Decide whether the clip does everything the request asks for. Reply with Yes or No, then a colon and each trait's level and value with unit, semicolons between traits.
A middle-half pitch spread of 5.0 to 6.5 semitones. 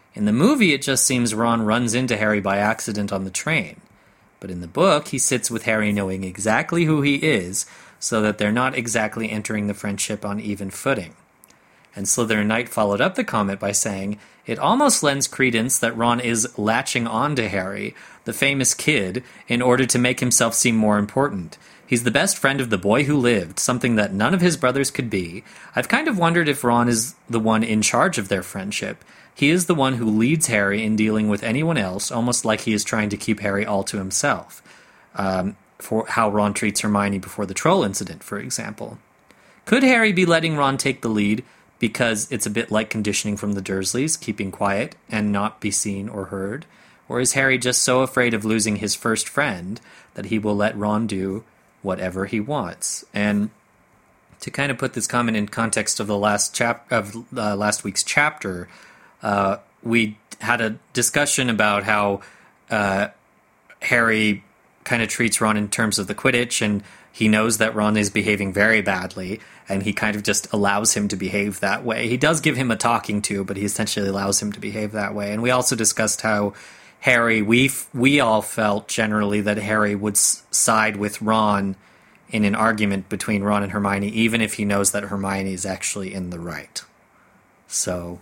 No: average, 3.0 semitones